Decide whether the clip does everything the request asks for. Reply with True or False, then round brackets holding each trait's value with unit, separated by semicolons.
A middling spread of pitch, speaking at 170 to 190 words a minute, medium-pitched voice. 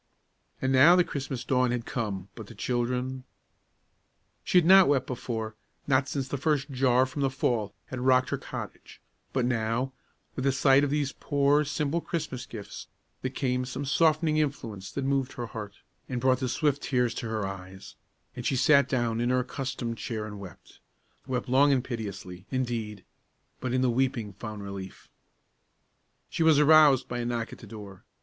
False (3.3 semitones; 180 wpm; 130 Hz)